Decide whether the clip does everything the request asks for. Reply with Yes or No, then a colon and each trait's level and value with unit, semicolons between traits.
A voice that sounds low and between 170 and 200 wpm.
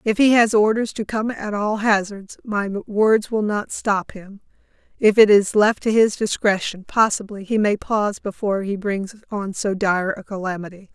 No: high, 205 Hz; average, 185 wpm